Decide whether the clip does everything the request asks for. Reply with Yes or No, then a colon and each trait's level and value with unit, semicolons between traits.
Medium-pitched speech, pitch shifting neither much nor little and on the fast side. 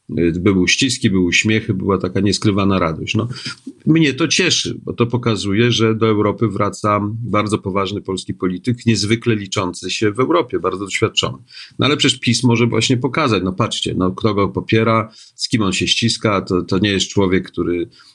No: low, 105 Hz; average, 3.6 semitones; fast, 180 wpm